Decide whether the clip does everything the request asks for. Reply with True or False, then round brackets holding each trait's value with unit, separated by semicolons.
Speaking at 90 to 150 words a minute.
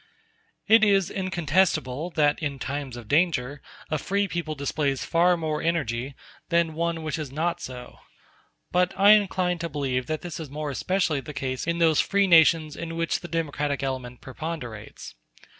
False (165 wpm)